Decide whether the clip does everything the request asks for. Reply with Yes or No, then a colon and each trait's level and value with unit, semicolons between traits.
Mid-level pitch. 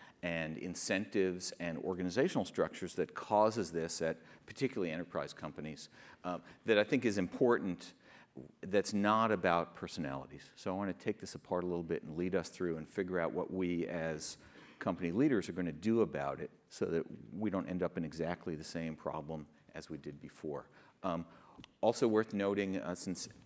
No: very low, 90 Hz